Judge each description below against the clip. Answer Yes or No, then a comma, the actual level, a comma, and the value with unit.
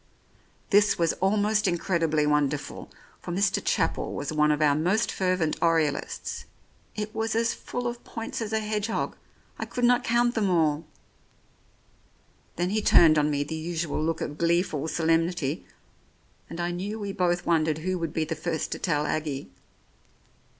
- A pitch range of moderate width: Yes, average, 4.7 semitones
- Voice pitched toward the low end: No, medium, 170 Hz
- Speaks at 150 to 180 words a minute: Yes, average, 160 wpm